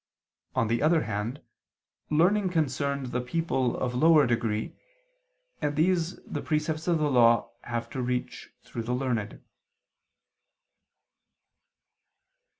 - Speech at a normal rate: No, slow, 115 wpm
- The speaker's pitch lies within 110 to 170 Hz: Yes, low, 135 Hz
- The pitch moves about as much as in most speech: Yes, average, 5.0 semitones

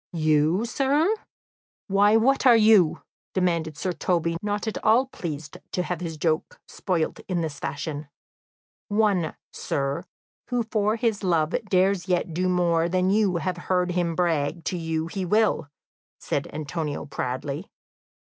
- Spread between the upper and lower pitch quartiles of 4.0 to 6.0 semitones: Yes, average, 4.4 semitones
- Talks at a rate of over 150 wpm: No, average, 145 wpm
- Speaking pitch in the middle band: Yes, medium, 180 Hz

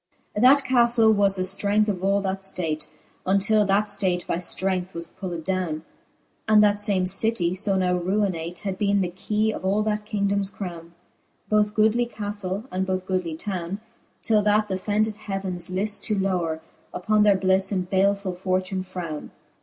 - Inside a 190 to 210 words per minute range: No, average, 170 wpm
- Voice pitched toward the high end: Yes, high, 195 Hz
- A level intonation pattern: Yes, narrow, 2.2 semitones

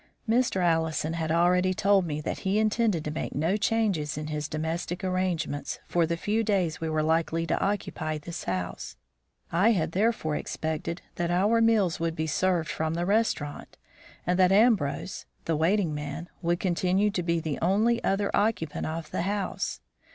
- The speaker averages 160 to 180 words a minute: Yes, average, 175 wpm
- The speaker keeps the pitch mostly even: No, average, 3.9 semitones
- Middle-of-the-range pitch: Yes, medium, 170 Hz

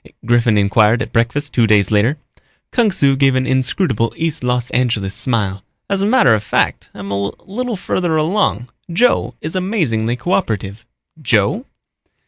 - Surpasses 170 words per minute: No, average, 150 wpm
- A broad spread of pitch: Yes, wide, 7.5 semitones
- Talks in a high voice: No, low, 125 Hz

